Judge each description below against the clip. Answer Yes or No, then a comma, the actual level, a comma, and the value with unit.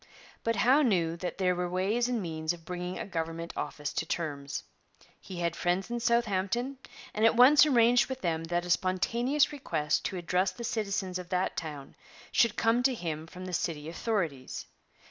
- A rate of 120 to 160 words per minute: No, average, 185 wpm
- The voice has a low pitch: No, medium, 185 Hz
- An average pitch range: No, wide, 5.7 semitones